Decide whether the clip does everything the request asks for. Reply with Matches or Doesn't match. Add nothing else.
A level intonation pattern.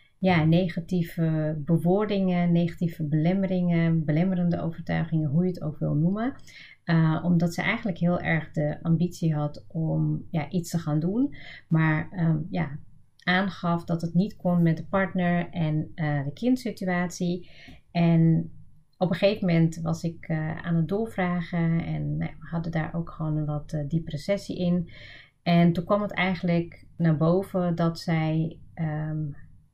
Matches